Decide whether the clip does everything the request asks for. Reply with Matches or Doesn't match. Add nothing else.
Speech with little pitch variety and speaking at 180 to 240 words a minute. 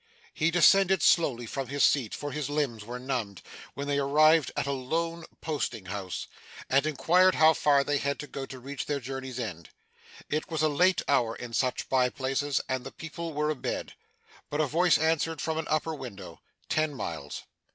Doesn't match